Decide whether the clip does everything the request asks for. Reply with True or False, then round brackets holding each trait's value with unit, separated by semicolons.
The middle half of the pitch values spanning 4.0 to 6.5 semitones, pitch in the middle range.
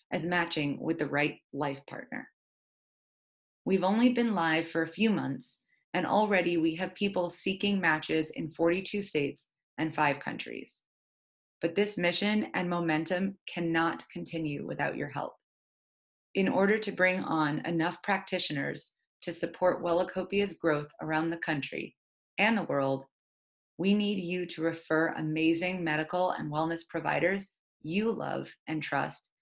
False (3.1 semitones; 170 Hz)